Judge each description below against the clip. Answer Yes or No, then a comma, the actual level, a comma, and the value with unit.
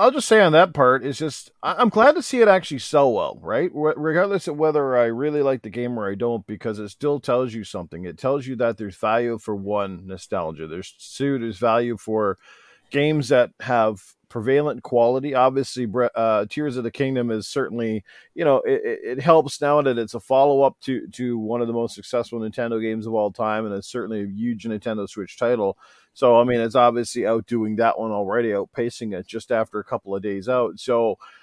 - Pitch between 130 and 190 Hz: No, low, 120 Hz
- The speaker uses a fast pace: Yes, fast, 210 wpm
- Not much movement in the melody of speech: No, average, 4.1 semitones